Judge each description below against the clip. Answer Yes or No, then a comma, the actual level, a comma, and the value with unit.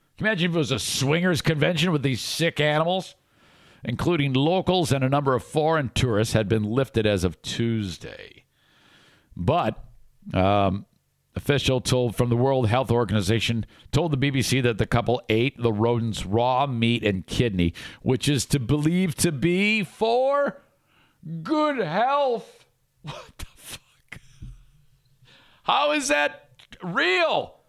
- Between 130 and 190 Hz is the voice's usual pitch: Yes, low, 135 Hz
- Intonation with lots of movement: Yes, wide, 5.8 semitones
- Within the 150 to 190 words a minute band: No, slow, 135 wpm